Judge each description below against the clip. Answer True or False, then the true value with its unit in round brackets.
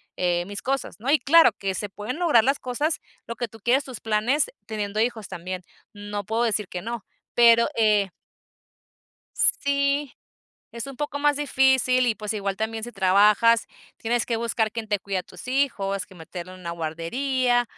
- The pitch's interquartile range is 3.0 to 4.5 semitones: True (4.2 semitones)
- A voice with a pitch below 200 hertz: False (225 Hz)